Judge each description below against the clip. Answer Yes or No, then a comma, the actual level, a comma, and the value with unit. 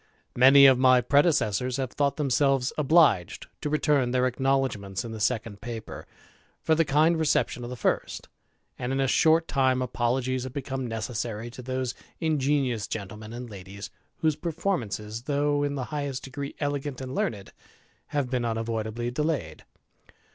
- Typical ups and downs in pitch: Yes, average, 3.5 semitones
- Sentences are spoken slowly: No, average, 160 wpm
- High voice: No, low, 130 Hz